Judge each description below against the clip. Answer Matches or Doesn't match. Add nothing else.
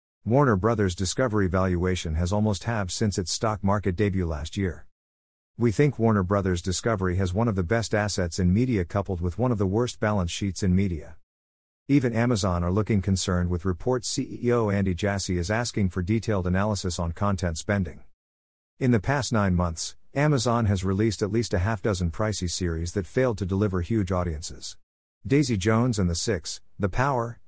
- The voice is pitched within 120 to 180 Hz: Doesn't match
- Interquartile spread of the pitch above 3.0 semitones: Matches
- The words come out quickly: Doesn't match